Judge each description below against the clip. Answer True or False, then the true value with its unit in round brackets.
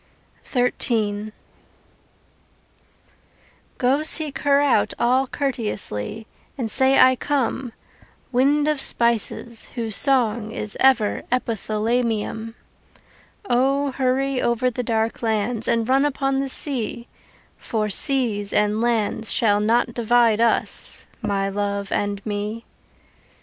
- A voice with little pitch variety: False (3.5 semitones)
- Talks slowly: True (110 wpm)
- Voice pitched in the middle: False (235 Hz)